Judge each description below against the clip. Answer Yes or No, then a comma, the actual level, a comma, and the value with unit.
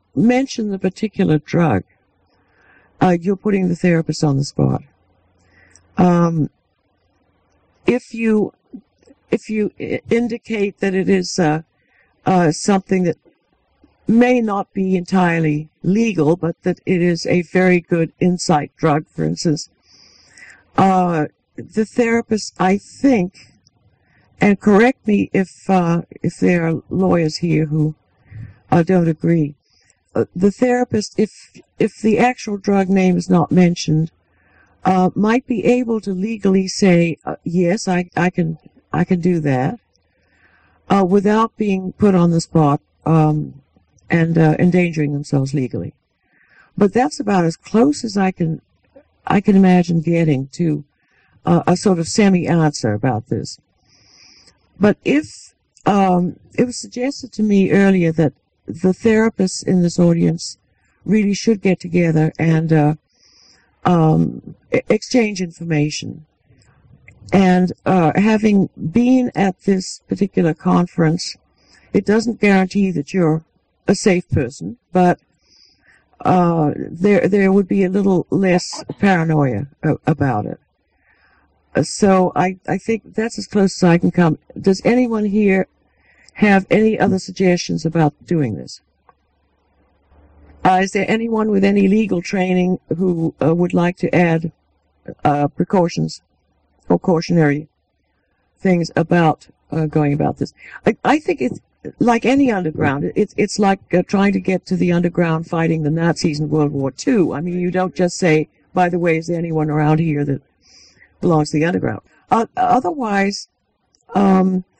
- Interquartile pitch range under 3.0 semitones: No, average, 4.4 semitones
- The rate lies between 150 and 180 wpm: No, average, 140 wpm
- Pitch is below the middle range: No, medium, 175 Hz